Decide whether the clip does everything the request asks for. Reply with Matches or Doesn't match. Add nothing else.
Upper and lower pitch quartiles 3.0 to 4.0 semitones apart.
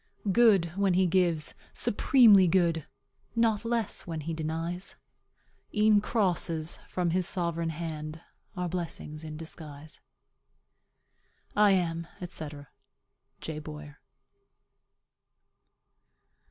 Matches